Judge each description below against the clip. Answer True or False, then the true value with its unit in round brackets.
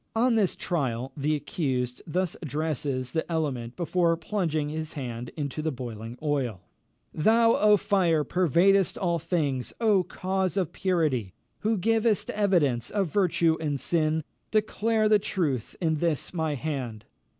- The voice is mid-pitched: True (160 Hz)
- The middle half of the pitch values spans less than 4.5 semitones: False (5.4 semitones)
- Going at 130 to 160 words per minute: True (145 wpm)